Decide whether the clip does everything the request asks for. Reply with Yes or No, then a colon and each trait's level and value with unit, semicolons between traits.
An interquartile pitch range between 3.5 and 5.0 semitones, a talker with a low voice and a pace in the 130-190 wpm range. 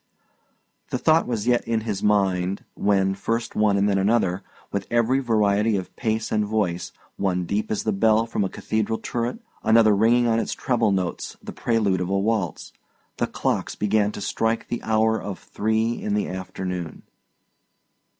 No: narrow, 2.6 semitones; low, 105 Hz; average, 170 wpm